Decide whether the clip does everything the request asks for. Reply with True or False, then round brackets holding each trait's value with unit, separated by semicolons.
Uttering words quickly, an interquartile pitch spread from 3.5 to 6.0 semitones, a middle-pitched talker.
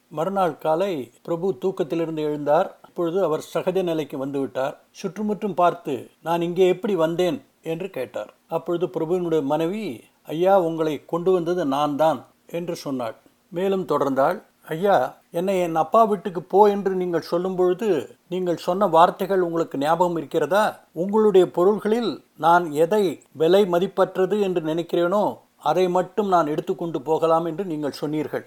False (135 wpm; 2.8 semitones; 175 Hz)